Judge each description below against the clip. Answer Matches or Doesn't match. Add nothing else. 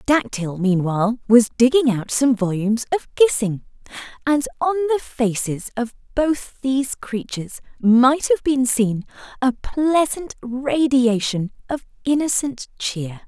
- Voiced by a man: Doesn't match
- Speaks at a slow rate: Matches